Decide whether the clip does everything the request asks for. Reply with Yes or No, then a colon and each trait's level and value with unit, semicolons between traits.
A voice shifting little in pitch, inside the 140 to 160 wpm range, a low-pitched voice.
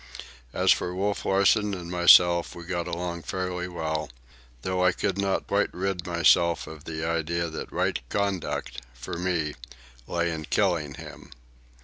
Yes: narrow, 1.8 semitones; average, 150 wpm; very low, 85 Hz